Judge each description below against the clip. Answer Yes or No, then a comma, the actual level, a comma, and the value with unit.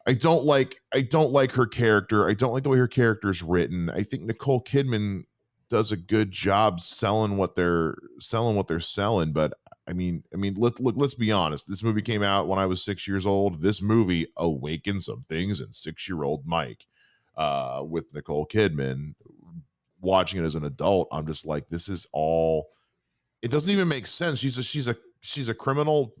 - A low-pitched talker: Yes, low, 100 Hz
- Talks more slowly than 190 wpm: No, average, 200 wpm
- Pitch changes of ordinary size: No, wide, 6.3 semitones